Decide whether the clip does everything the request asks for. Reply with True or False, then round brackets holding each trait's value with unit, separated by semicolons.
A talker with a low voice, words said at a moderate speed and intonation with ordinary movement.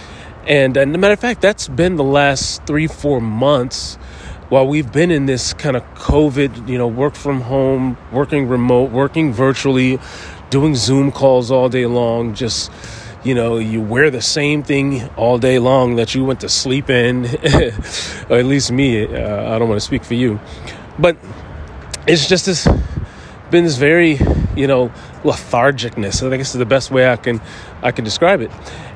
True (130 Hz; 180 wpm; 3.7 semitones)